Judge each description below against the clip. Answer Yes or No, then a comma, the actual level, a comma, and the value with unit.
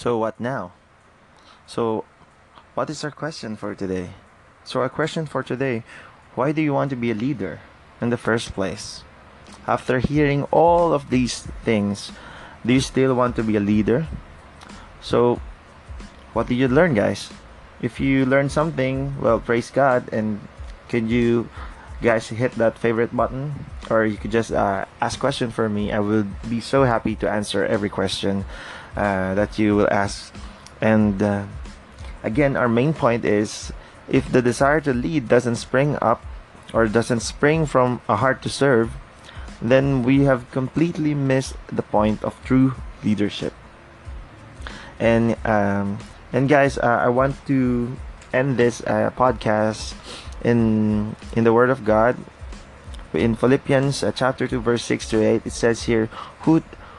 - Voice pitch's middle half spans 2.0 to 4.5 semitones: Yes, average, 3.8 semitones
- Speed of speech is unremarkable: No, fast, 160 wpm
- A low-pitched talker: Yes, low, 115 Hz